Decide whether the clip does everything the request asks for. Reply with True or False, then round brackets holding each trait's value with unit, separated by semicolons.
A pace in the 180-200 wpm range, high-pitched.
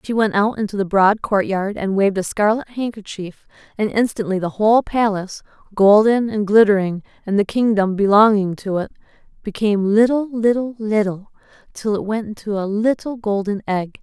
False (165 wpm; 210 Hz)